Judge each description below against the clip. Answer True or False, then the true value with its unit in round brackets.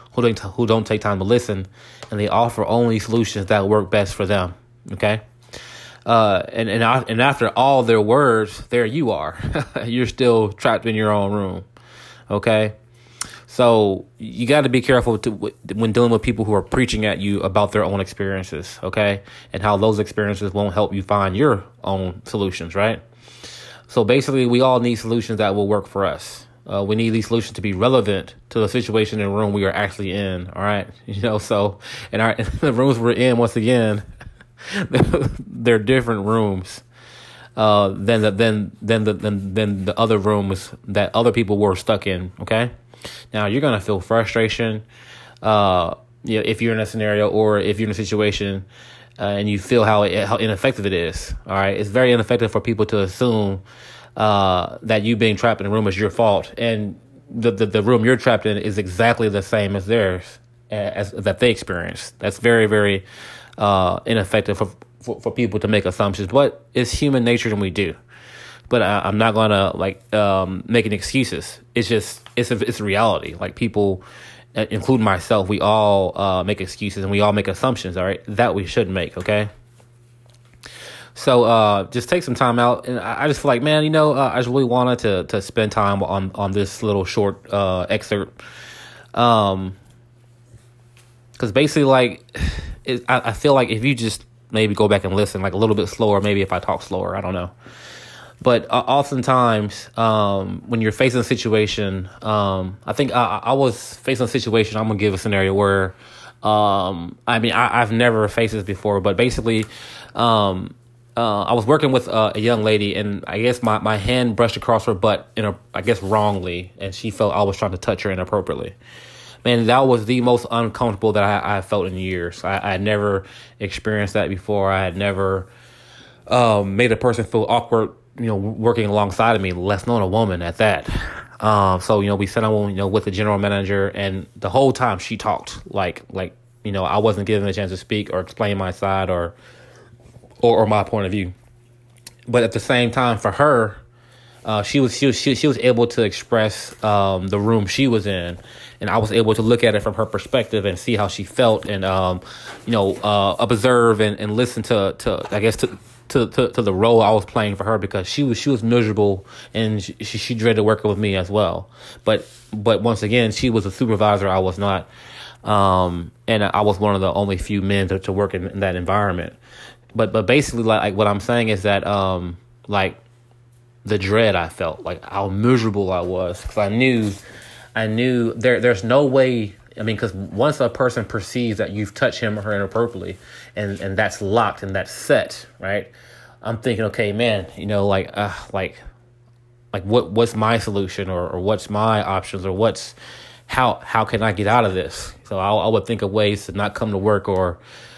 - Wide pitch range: False (2.9 semitones)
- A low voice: True (110 Hz)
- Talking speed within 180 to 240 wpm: True (205 wpm)